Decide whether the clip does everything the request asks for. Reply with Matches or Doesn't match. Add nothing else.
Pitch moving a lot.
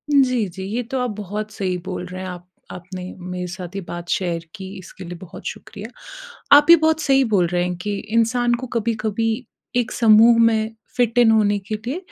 Doesn't match